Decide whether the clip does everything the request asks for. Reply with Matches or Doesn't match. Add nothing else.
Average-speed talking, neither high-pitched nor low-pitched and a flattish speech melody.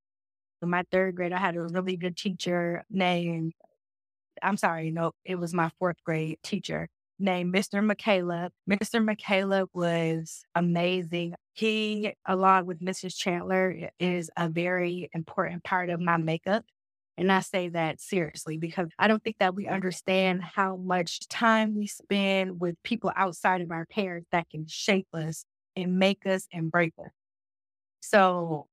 Matches